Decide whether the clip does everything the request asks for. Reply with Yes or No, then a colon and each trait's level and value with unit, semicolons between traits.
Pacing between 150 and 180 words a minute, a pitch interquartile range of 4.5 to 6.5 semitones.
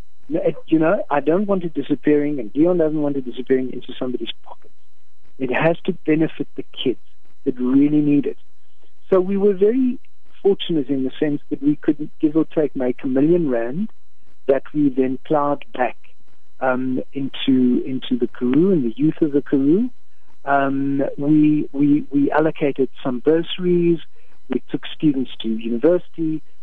No: average, 165 wpm; average, 3.6 semitones